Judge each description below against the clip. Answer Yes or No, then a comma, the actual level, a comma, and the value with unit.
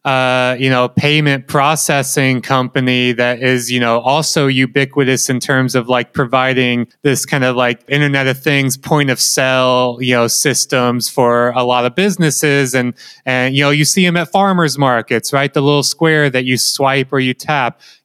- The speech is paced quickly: No, average, 185 wpm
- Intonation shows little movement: Yes, narrow, 2.3 semitones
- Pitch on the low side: Yes, low, 130 Hz